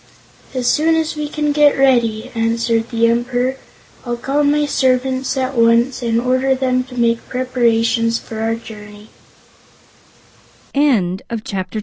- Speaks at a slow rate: Yes, slow, 125 wpm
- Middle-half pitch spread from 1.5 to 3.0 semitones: Yes, narrow, 2.5 semitones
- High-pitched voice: Yes, very high, 250 Hz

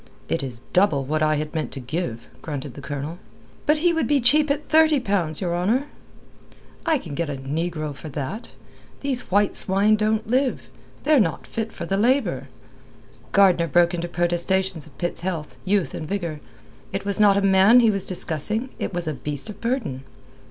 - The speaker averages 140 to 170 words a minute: No, average, 185 wpm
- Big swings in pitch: Yes, wide, 6.0 semitones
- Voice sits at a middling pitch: Yes, medium, 180 Hz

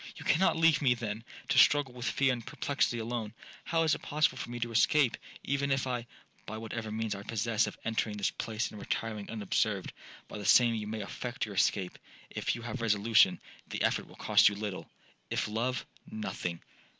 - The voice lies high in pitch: No, low, 115 Hz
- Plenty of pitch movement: No, average, 3.2 semitones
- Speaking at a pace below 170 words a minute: No, average, 180 wpm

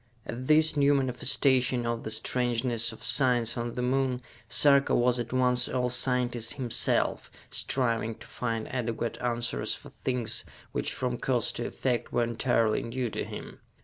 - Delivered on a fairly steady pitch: Yes, narrow, 1.6 semitones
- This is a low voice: Yes, low, 125 Hz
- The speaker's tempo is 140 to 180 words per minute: Yes, average, 155 wpm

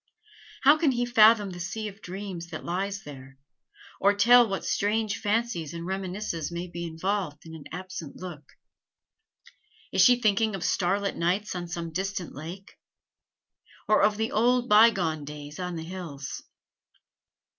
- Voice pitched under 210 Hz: Yes, high, 190 Hz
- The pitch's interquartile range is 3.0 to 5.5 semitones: Yes, average, 4.0 semitones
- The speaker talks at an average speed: Yes, average, 150 wpm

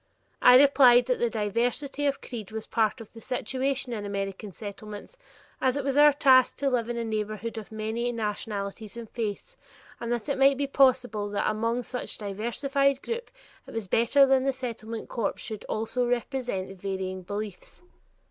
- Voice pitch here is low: No, high, 235 Hz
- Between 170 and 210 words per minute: Yes, average, 175 wpm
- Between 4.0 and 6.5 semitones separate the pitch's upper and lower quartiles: No, average, 3.6 semitones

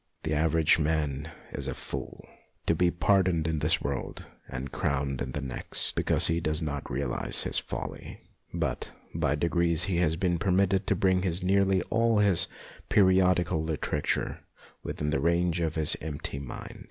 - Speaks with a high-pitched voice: No, very low, 80 Hz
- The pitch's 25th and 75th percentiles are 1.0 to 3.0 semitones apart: No, average, 3.6 semitones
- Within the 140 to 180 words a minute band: Yes, average, 165 wpm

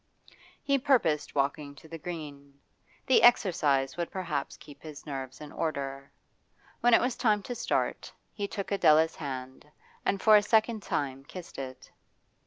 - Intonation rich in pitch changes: Yes, wide, 6.6 semitones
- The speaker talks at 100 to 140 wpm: No, average, 155 wpm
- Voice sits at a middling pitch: Yes, medium, 155 Hz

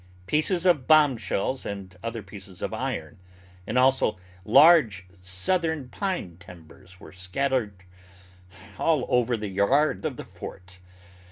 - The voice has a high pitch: No, low, 115 Hz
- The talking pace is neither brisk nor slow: No, slow, 120 wpm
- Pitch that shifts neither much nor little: No, wide, 7.7 semitones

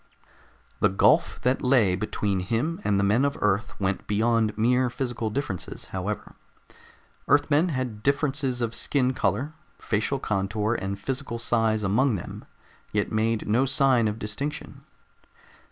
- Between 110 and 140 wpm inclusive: Yes, slow, 135 wpm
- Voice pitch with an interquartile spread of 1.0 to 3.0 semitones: No, average, 4.2 semitones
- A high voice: No, low, 115 Hz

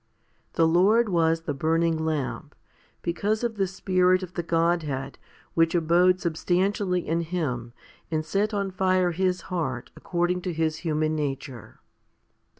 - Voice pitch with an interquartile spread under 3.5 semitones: Yes, narrow, 2.6 semitones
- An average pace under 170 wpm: Yes, average, 140 wpm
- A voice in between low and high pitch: Yes, medium, 170 Hz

